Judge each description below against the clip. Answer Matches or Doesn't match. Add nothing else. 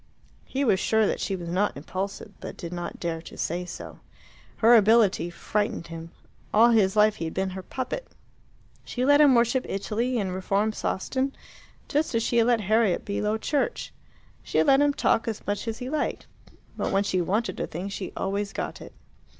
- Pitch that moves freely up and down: Doesn't match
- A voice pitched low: Doesn't match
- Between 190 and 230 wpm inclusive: Matches